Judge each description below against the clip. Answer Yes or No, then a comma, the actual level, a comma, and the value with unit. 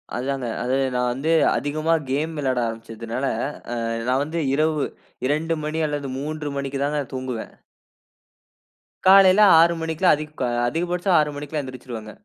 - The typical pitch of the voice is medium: Yes, medium, 145 Hz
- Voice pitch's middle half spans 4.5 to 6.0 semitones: No, average, 3.7 semitones